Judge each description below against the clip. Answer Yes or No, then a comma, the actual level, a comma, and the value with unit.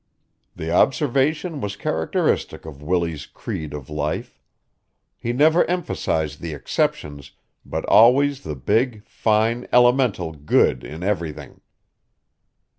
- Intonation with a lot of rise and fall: Yes, wide, 8.7 semitones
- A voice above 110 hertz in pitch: No, very low, 95 Hz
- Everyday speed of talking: No, slow, 110 wpm